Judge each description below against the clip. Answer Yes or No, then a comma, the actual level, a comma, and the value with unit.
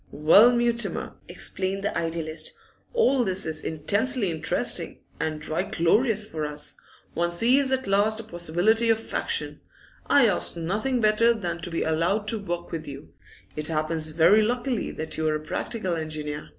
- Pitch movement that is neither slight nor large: No, wide, 5.8 semitones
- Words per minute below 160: No, average, 165 wpm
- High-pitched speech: No, medium, 180 Hz